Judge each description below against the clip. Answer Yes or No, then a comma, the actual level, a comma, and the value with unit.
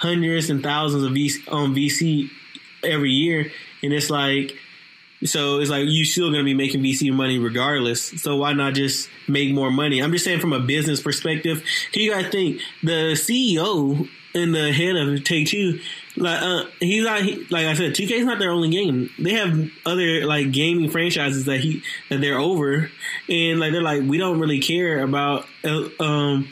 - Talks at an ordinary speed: Yes, average, 190 wpm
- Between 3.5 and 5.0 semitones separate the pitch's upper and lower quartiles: No, average, 3.1 semitones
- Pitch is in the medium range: Yes, medium, 150 Hz